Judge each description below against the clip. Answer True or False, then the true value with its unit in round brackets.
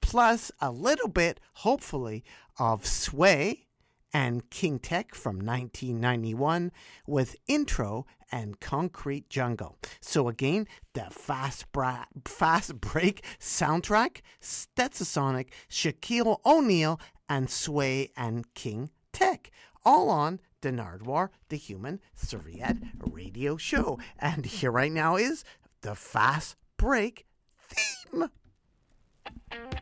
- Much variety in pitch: True (7.2 semitones)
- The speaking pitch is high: False (145 Hz)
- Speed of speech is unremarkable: False (105 wpm)